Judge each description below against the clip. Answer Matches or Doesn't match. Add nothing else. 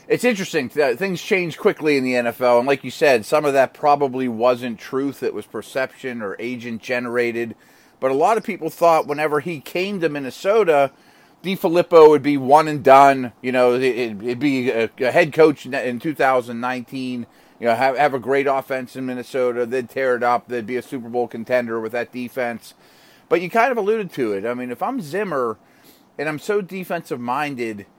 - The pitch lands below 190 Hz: Matches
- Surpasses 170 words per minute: Matches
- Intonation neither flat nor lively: Matches